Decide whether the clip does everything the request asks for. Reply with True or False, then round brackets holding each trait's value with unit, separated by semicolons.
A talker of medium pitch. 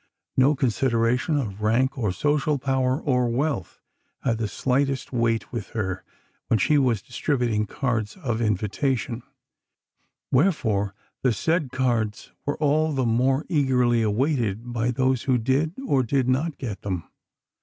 False (125 Hz)